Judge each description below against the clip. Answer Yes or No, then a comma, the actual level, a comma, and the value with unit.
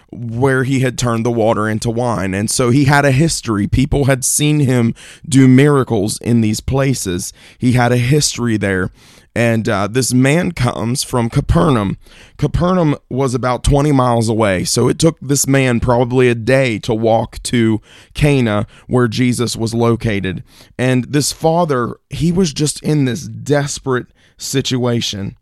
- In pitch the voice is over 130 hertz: No, low, 125 Hz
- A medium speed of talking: Yes, average, 160 wpm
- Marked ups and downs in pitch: No, average, 3.1 semitones